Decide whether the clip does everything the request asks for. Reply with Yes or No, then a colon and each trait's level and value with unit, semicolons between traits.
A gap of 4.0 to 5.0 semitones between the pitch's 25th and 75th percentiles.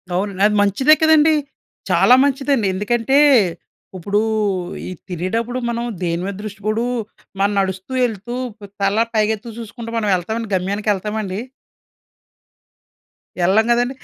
No: average, 3.1 semitones